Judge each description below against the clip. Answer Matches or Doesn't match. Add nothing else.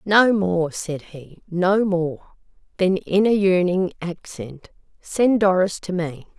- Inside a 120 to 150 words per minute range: Matches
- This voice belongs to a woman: Matches